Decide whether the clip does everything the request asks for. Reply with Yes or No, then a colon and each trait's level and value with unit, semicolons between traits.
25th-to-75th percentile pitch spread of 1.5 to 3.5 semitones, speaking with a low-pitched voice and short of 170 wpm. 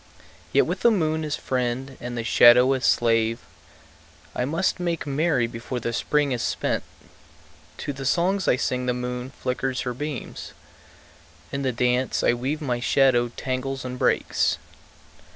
Yes: average, 2.7 semitones; low, 130 Hz; average, 155 wpm